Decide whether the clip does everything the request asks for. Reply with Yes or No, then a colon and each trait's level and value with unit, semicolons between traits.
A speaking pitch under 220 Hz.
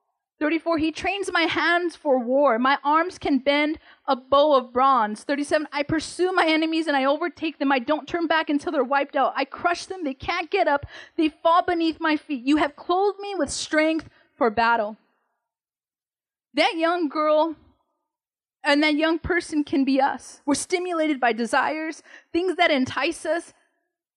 No: very high, 310 Hz